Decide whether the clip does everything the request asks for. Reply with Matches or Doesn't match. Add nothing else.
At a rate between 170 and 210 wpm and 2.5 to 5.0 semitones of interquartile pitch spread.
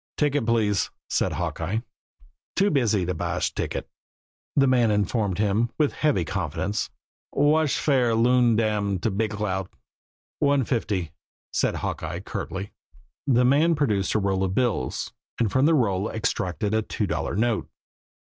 Doesn't match